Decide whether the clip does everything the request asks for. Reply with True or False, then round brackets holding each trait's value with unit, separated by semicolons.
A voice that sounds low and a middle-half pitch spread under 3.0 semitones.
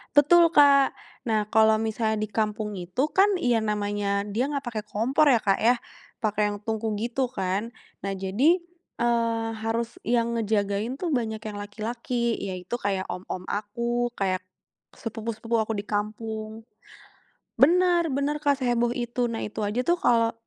False (225 Hz; 2.6 semitones)